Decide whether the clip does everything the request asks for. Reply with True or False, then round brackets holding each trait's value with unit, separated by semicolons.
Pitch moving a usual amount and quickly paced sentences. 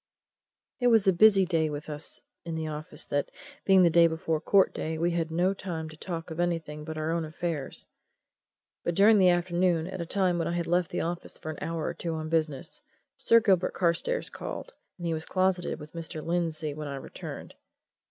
False (2.3 semitones; 210 wpm)